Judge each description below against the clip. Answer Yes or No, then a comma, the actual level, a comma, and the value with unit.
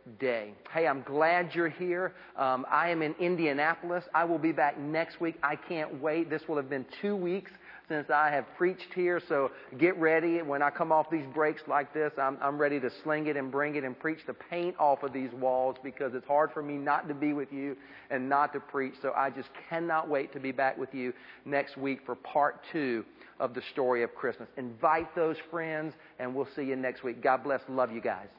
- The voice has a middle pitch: Yes, medium, 150 Hz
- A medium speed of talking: No, fast, 225 wpm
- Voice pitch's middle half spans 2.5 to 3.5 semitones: Yes, average, 3.2 semitones